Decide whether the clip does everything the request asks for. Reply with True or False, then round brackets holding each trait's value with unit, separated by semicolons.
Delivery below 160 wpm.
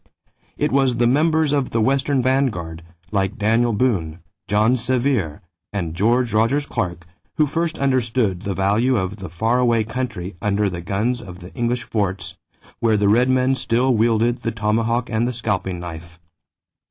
False (165 wpm)